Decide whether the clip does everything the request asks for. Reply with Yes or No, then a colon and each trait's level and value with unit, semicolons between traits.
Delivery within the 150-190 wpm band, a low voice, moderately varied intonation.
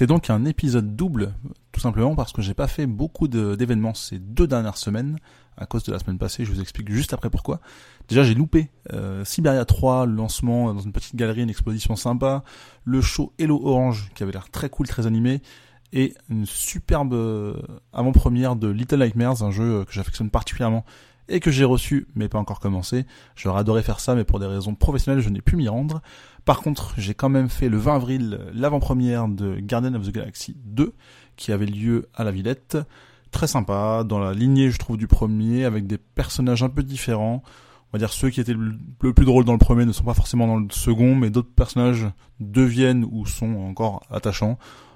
No: average, 205 wpm; low, 120 Hz; average, 3.5 semitones